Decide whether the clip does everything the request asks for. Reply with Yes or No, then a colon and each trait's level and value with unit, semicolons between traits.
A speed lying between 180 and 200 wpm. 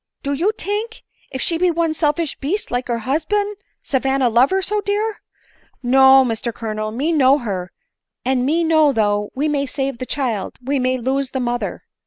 Yes: average, 190 wpm